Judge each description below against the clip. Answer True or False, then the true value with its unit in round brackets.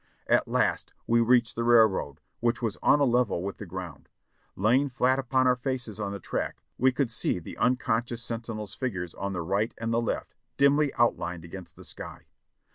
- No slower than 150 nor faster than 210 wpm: True (190 wpm)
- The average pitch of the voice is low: True (115 Hz)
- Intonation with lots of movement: False (4.1 semitones)